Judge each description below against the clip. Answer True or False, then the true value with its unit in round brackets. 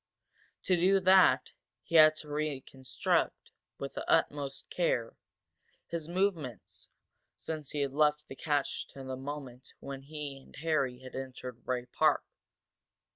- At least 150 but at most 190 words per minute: False (135 wpm)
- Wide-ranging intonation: False (2.9 semitones)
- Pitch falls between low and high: True (145 Hz)